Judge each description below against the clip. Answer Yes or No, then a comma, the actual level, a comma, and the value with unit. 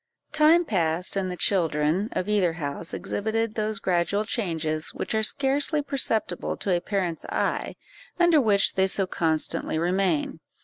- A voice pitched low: No, high, 195 Hz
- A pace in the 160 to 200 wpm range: No, average, 145 wpm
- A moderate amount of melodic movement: Yes, average, 4.5 semitones